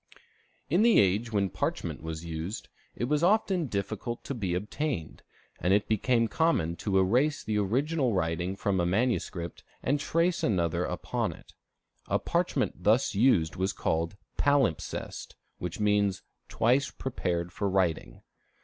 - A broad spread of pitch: Yes, wide, 6.7 semitones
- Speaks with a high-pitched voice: No, low, 105 Hz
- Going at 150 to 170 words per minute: No, average, 140 wpm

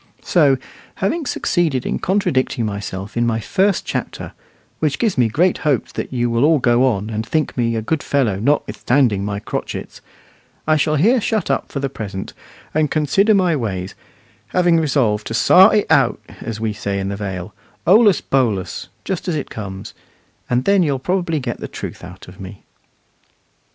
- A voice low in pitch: Yes, low, 130 Hz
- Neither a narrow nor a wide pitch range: No, wide, 7.7 semitones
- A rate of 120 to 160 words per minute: No, average, 175 wpm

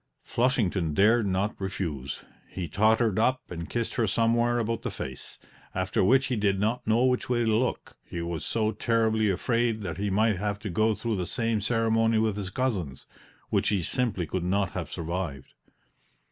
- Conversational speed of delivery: Yes, average, 180 wpm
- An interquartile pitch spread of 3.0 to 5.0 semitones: Yes, average, 3.7 semitones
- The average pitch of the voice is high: No, low, 110 Hz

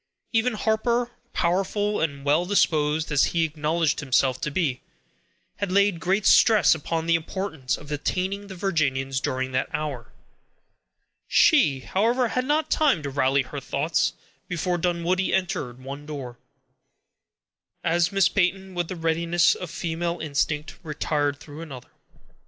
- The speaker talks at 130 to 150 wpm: Yes, average, 140 wpm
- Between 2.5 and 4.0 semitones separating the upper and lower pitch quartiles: No, average, 4.8 semitones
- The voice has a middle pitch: Yes, medium, 165 Hz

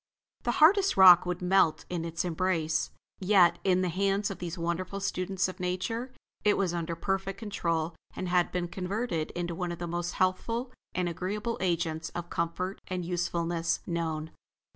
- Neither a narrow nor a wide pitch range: No, narrow, 2.2 semitones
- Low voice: No, medium, 180 Hz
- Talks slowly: No, average, 165 wpm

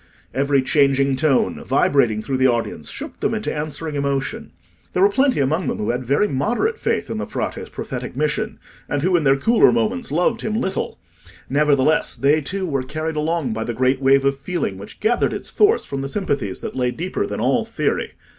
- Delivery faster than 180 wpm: Yes, average, 195 wpm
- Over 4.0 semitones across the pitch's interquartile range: Yes, average, 5.3 semitones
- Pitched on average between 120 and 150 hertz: Yes, medium, 140 Hz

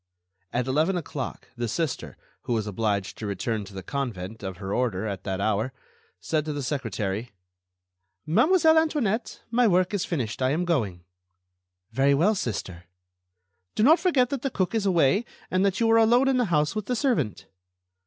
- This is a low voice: No, medium, 145 Hz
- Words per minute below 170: No, average, 180 wpm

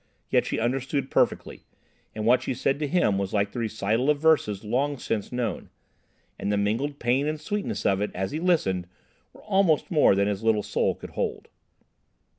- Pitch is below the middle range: Yes, low, 120 Hz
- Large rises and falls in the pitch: Yes, wide, 6.0 semitones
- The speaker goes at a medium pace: Yes, average, 190 wpm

